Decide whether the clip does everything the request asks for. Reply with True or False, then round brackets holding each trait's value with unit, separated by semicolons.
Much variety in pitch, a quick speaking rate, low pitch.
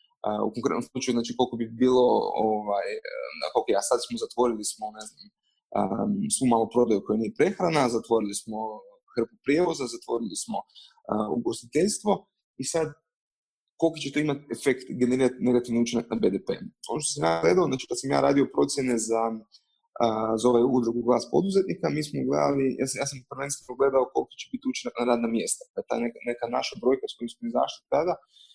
True (8.6 semitones; 185 wpm; 130 Hz)